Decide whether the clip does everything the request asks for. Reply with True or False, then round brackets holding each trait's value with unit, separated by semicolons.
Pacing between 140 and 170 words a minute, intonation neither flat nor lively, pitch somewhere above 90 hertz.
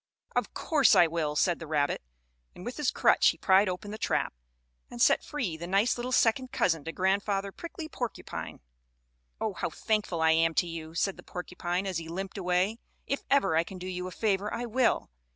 False (205 wpm; 4.7 semitones; 190 Hz)